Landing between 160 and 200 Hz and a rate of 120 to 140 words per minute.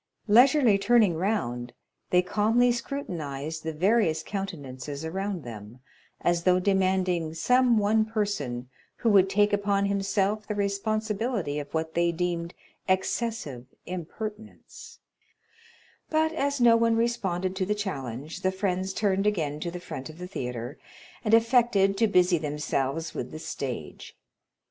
Yes: high, 190 Hz; slow, 135 wpm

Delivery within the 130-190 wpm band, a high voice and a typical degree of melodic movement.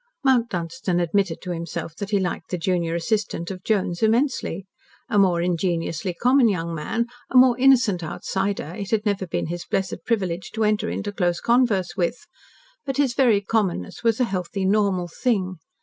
Yes: average, 175 wpm; high, 195 Hz; average, 4.4 semitones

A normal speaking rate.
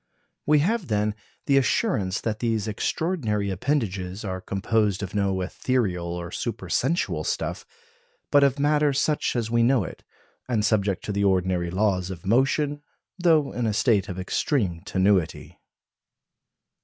Yes: average, 145 wpm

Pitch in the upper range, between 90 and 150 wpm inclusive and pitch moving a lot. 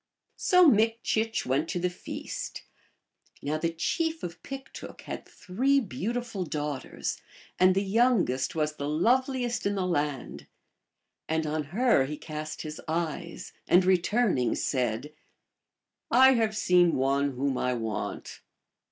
No: medium, 175 Hz; average, 140 wpm; wide, 7.3 semitones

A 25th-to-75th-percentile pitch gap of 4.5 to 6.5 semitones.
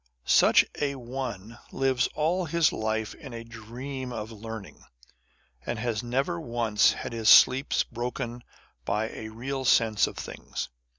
No: average, 3.2 semitones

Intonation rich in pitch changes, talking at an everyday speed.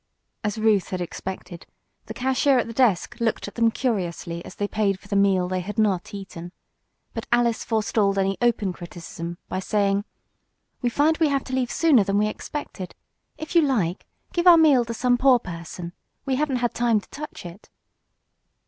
No: average, 4.9 semitones; average, 185 wpm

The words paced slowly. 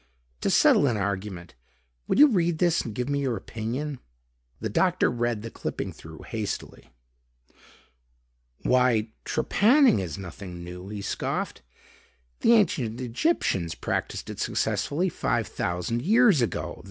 Yes: slow, 130 wpm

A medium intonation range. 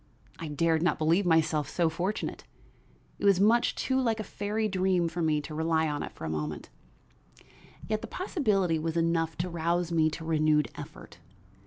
Yes: average, 3.4 semitones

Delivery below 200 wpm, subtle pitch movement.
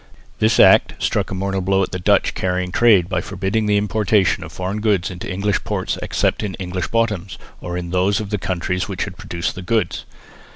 No: fast, 205 wpm; narrow, 2.3 semitones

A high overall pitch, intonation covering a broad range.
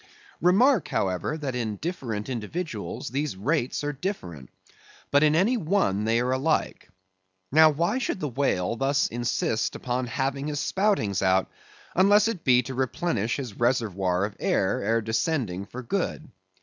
No: low, 130 Hz; wide, 6.2 semitones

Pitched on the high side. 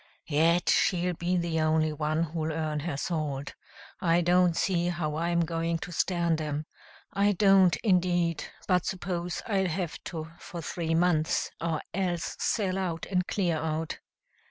No: medium, 170 Hz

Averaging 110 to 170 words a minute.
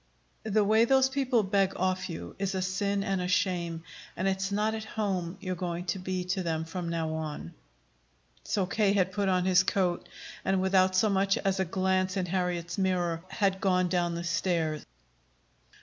No: average, 185 wpm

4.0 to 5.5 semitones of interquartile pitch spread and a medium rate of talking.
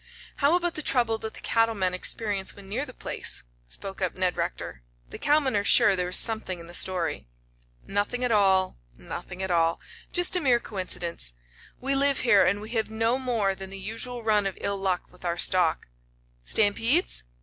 Yes: average, 4.3 semitones; average, 195 wpm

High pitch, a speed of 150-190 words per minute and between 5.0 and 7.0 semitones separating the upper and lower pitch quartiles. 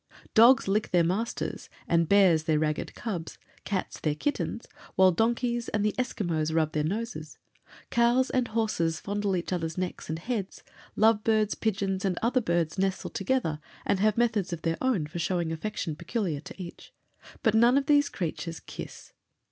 Yes: high, 195 Hz; average, 170 wpm; average, 5.3 semitones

